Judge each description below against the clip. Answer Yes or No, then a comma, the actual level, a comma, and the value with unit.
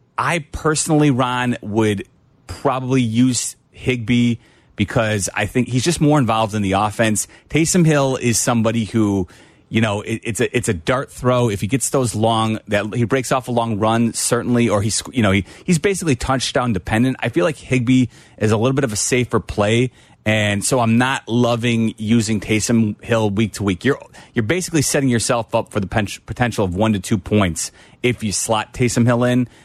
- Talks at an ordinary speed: Yes, average, 195 wpm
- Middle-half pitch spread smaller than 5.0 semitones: Yes, average, 2.9 semitones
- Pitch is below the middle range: Yes, low, 115 Hz